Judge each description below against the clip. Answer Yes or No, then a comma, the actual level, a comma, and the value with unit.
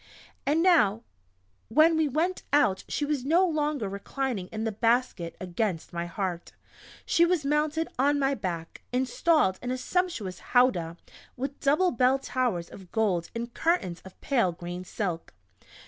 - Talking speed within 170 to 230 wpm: No, average, 150 wpm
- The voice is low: No, high, 245 Hz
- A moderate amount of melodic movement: No, wide, 7.9 semitones